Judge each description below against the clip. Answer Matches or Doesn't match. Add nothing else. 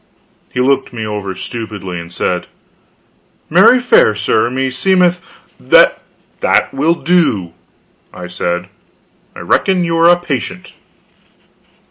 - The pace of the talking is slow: Matches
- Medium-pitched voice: Doesn't match